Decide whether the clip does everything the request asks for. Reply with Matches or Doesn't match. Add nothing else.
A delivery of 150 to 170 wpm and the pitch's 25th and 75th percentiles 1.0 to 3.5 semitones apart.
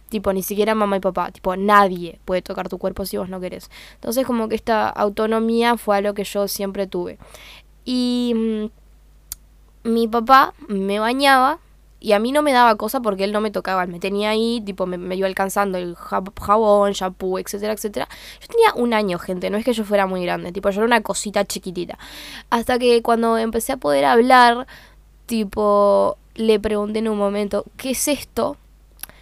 Doesn't match